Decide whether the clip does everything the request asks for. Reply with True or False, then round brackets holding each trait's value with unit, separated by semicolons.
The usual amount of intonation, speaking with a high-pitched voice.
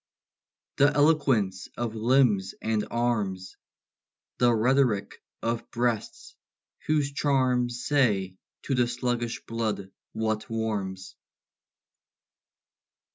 False (3.1 semitones; 115 Hz)